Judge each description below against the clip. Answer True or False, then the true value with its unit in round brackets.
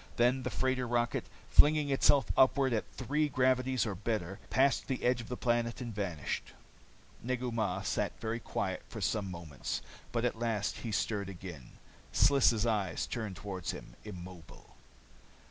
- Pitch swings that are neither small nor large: True (4.2 semitones)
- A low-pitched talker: True (115 Hz)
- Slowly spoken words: False (155 wpm)